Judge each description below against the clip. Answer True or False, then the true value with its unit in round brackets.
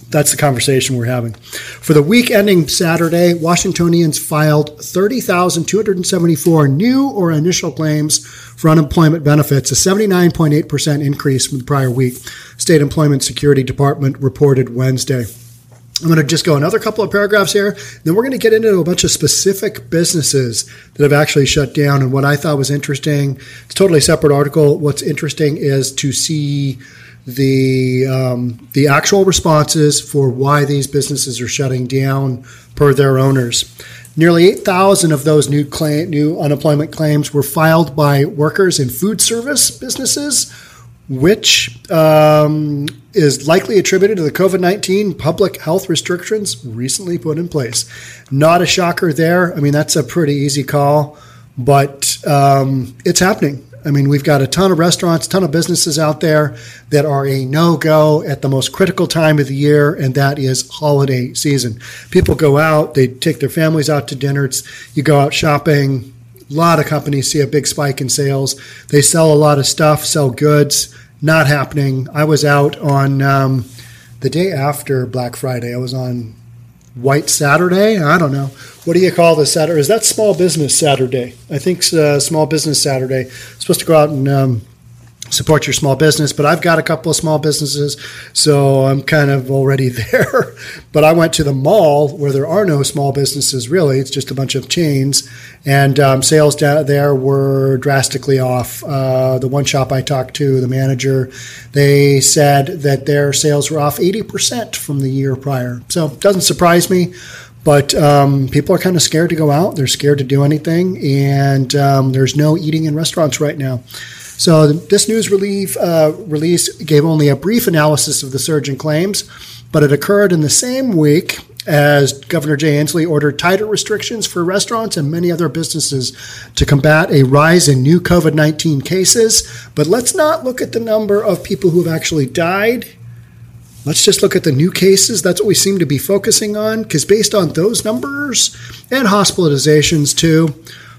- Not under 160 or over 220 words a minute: True (180 wpm)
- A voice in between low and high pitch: True (150 Hz)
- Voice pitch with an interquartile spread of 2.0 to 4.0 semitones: True (3.6 semitones)